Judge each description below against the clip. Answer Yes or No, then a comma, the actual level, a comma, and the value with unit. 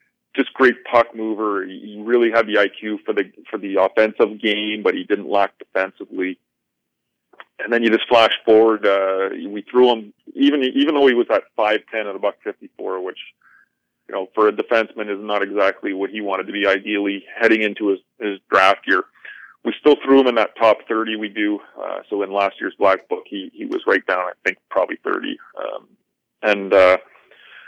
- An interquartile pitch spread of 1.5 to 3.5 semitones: Yes, average, 2.9 semitones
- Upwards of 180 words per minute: Yes, average, 195 wpm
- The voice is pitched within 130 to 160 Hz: No, low, 110 Hz